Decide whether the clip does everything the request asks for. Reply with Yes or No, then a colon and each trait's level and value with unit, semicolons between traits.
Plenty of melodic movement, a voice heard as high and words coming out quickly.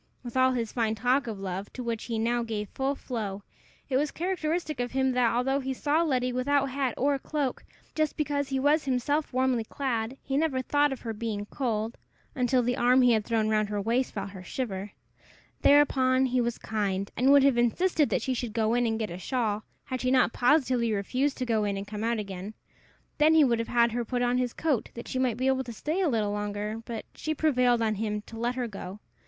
No: average, 3.4 semitones; high, 245 Hz; fast, 230 wpm